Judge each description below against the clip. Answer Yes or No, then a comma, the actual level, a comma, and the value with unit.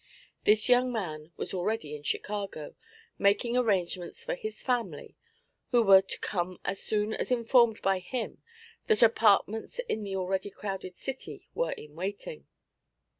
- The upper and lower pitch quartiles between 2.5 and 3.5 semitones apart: No, average, 3.9 semitones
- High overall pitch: Yes, high, 205 Hz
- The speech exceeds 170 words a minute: No, average, 145 wpm